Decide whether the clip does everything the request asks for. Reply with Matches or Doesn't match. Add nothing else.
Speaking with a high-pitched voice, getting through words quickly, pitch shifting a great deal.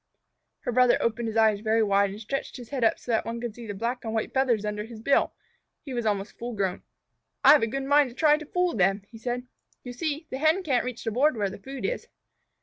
Doesn't match